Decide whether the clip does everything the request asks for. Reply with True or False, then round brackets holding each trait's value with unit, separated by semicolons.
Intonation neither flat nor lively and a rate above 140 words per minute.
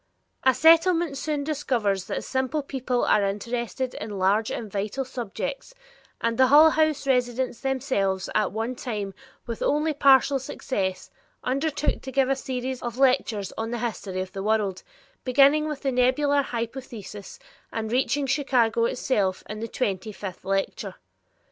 True (4.4 semitones; 150 wpm)